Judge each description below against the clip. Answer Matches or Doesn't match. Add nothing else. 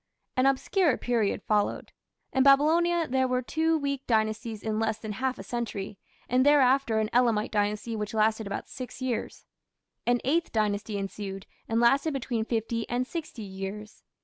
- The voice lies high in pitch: Matches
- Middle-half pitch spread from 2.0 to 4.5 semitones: Matches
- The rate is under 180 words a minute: Matches